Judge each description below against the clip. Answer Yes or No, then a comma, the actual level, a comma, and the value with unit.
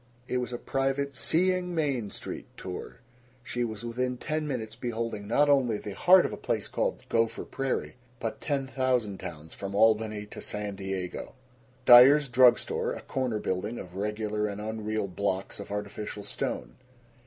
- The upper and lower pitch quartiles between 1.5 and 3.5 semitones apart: No, average, 4.2 semitones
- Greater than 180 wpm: No, average, 165 wpm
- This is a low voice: Yes, low, 115 Hz